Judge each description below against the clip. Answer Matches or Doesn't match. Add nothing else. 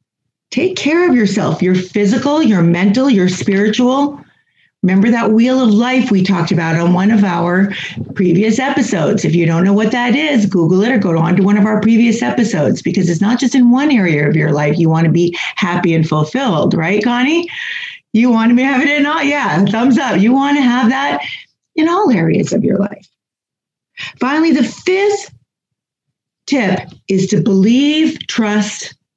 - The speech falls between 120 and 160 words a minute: Doesn't match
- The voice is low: Doesn't match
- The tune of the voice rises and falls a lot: Matches